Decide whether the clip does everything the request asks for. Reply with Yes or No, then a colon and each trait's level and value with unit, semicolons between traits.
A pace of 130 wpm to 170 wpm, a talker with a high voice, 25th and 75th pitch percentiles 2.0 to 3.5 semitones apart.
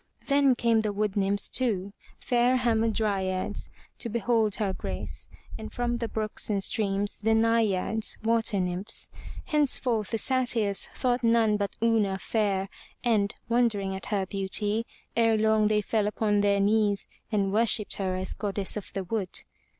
Yes: average, 160 wpm; high, 215 Hz; narrow, 2.4 semitones